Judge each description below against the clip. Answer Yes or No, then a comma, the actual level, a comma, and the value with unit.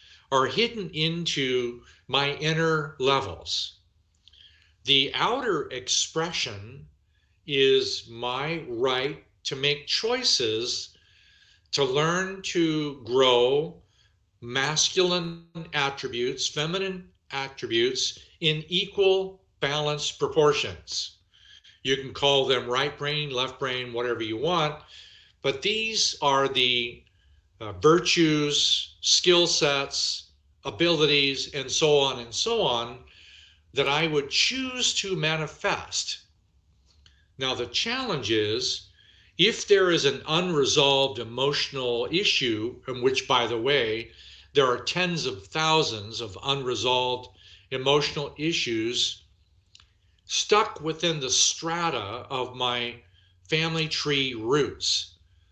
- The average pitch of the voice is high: No, low, 135 Hz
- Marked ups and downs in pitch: Yes, wide, 6.3 semitones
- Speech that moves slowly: Yes, slow, 100 wpm